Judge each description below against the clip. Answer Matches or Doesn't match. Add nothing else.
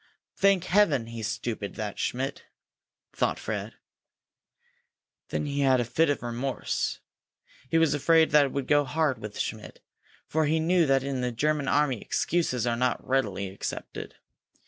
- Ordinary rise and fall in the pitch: Matches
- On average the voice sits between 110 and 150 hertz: Matches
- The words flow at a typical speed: Matches